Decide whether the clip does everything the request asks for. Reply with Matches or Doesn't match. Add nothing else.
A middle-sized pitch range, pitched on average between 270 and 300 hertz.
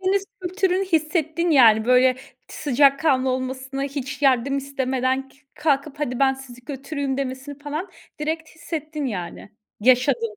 Matches